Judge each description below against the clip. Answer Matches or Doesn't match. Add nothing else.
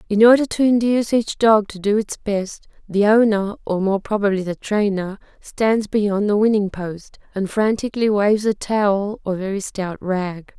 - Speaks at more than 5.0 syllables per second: Doesn't match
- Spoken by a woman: Matches